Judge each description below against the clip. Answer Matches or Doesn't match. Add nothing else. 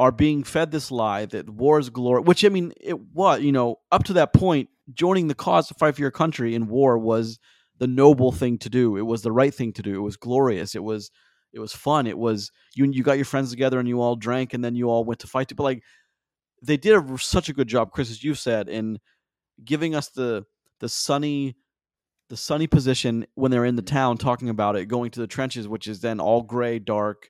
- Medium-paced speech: Doesn't match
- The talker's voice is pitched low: Matches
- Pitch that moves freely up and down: Doesn't match